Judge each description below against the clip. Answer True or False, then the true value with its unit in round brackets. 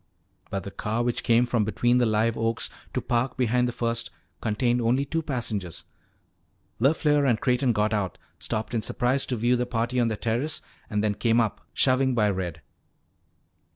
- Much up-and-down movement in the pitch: False (2.4 semitones)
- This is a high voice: False (120 Hz)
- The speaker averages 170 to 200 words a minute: True (180 wpm)